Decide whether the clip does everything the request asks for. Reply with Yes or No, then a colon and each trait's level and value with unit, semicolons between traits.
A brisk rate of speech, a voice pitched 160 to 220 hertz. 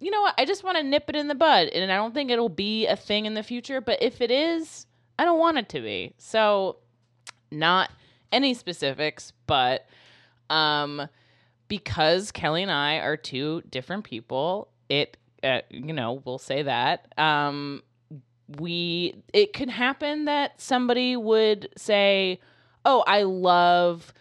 No: average, 165 wpm; medium, 185 Hz